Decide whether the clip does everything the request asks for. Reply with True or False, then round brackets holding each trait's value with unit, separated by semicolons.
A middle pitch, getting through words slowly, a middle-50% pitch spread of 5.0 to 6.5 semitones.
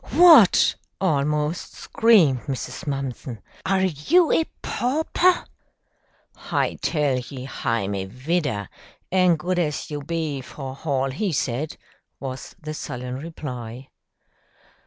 True (145 Hz; 115 wpm; 5.4 semitones)